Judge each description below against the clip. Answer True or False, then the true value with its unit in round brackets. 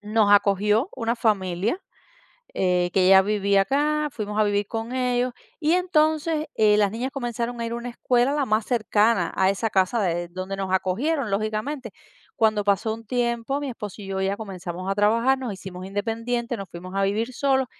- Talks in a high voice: True (215 Hz)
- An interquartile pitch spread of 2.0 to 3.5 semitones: False (3.9 semitones)